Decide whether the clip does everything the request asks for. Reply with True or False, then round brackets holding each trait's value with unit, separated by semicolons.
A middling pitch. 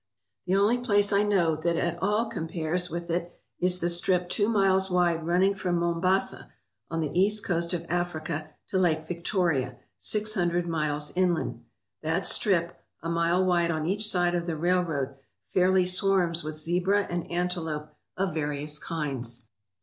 True (175 Hz)